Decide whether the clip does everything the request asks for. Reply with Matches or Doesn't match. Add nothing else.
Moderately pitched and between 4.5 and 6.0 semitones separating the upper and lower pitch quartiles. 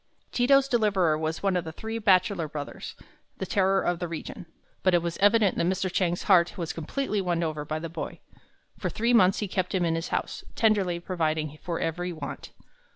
Doesn't match